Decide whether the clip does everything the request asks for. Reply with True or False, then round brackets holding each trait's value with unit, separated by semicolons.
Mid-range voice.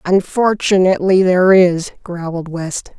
True (180 Hz)